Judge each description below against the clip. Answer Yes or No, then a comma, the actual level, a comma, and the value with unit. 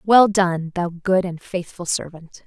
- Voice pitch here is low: No, medium, 180 Hz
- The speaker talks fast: No, average, 170 wpm